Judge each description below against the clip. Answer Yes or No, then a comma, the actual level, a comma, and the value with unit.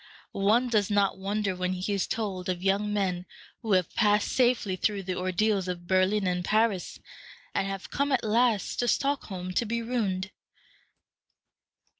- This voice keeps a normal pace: Yes, average, 160 wpm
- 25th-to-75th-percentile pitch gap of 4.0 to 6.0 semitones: No, average, 2.9 semitones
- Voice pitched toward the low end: No, high, 200 Hz